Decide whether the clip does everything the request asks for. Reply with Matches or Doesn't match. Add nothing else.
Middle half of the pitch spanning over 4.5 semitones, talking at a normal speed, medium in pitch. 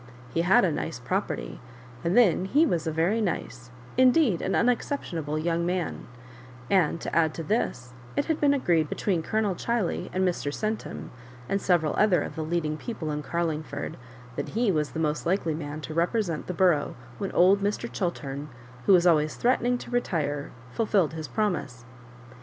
Matches